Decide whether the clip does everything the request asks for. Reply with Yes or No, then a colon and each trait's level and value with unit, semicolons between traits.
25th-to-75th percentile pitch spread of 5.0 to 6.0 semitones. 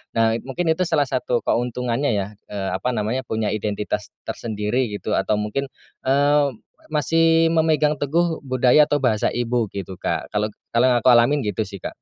Yes: wide, 5.4 semitones